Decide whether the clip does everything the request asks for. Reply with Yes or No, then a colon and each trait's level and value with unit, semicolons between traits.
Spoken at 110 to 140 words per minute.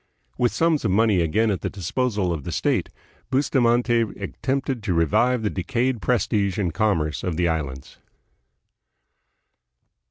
Yes: slow, 135 wpm